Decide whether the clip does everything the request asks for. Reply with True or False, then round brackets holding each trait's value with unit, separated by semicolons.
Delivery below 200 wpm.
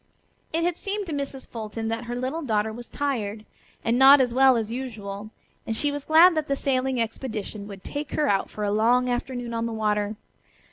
False (205 wpm)